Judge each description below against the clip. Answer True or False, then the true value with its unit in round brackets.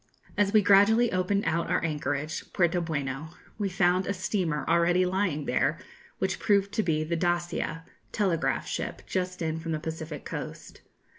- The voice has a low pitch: False (175 Hz)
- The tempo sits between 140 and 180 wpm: True (165 wpm)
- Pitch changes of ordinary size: True (3.3 semitones)